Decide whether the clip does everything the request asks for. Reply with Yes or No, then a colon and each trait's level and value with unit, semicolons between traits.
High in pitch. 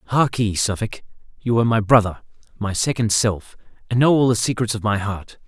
No: low, 110 Hz